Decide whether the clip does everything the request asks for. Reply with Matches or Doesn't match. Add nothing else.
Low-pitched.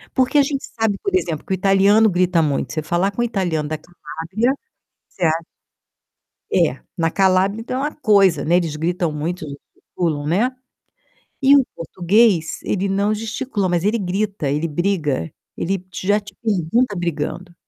Doesn't match